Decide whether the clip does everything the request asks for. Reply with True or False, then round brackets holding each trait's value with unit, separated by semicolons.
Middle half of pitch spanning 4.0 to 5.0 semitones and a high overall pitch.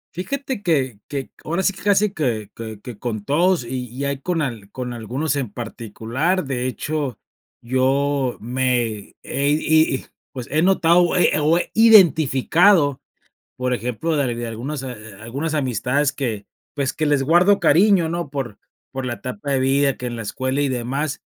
False (4.5 semitones; 135 Hz)